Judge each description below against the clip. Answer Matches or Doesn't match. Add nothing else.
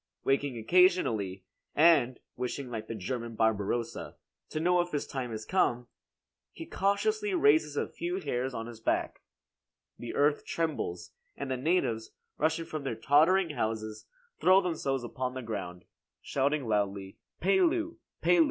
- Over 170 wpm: Doesn't match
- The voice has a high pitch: Doesn't match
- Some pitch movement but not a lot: Doesn't match